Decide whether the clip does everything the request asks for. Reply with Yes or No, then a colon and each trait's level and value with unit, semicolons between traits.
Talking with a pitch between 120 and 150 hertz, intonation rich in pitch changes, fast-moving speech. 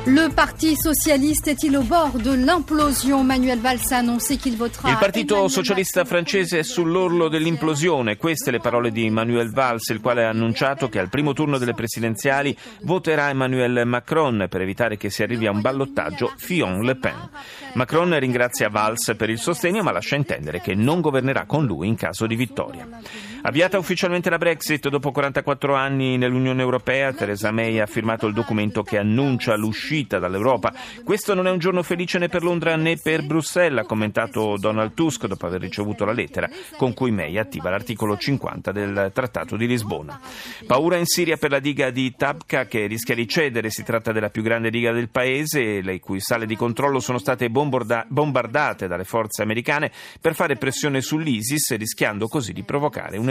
Yes: low, 130 Hz; wide, 6.5 semitones; fast, 175 wpm